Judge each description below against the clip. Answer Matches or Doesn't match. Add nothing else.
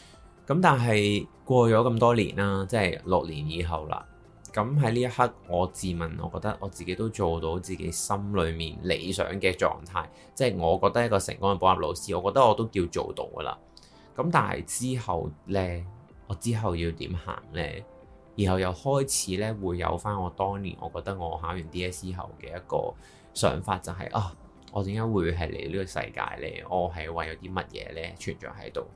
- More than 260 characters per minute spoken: Matches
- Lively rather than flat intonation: Doesn't match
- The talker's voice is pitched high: Doesn't match